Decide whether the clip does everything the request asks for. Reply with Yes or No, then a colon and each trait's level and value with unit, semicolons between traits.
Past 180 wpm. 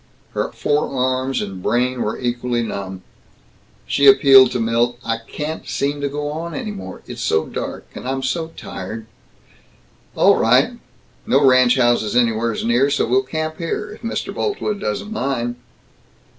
No: average, 155 wpm